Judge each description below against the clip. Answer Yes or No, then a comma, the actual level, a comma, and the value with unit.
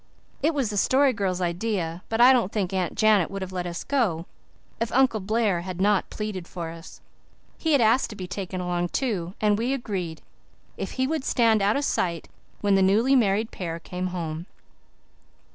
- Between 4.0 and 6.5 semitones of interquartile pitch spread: Yes, average, 4.4 semitones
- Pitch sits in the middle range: No, high, 200 Hz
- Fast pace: No, average, 190 wpm